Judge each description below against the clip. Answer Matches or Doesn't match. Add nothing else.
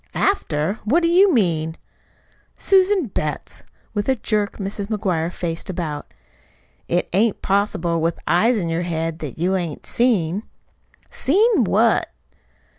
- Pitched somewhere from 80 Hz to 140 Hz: Doesn't match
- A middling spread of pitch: Doesn't match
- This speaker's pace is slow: Matches